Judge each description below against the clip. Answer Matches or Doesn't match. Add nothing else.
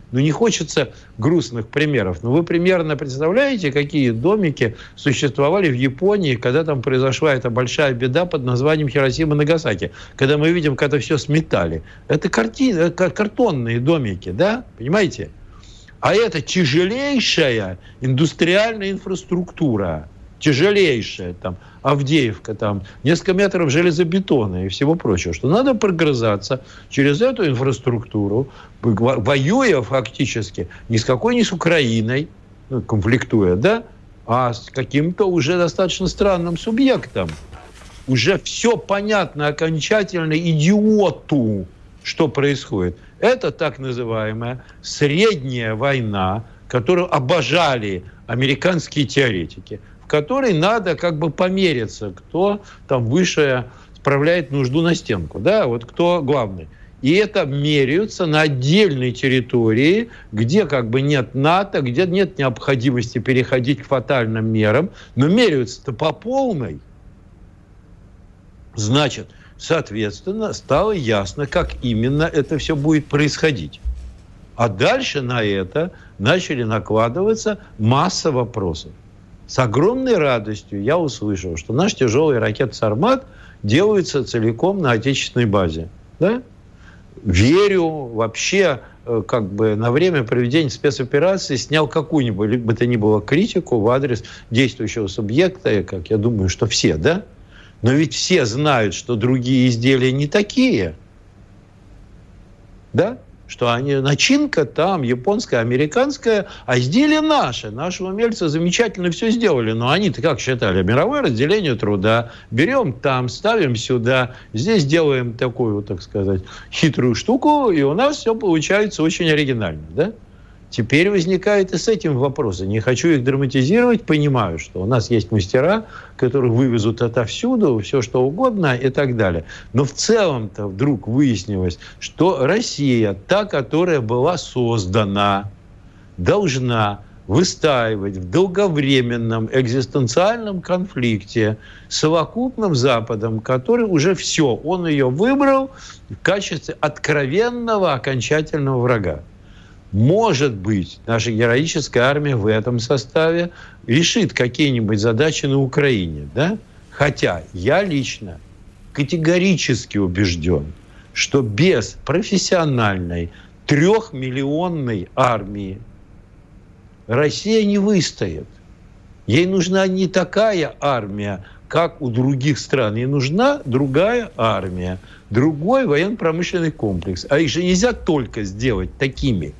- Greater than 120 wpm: Doesn't match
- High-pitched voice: Doesn't match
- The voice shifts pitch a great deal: Matches